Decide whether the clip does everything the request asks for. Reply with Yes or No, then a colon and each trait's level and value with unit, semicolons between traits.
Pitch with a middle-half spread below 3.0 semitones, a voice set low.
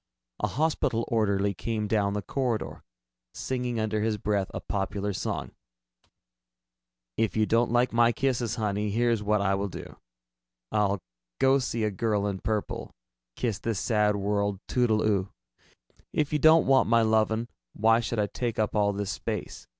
Yes: narrow, 2.5 semitones; low, 110 Hz